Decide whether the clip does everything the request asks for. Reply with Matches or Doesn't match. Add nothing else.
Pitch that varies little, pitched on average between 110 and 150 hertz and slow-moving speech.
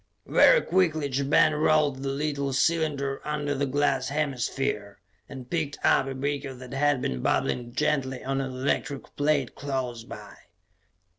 Doesn't match